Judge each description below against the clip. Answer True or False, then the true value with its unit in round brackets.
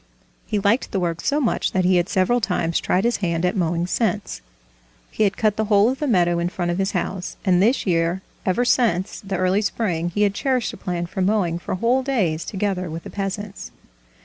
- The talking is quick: True (220 wpm)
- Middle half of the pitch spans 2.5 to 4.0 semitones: True (3.4 semitones)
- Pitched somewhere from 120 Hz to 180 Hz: False (190 Hz)